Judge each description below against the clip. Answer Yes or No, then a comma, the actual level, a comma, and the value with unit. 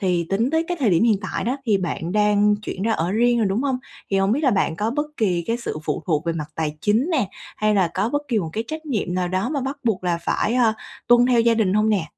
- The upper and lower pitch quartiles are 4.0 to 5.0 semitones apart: Yes, average, 4.7 semitones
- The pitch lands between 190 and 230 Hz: Yes, high, 210 Hz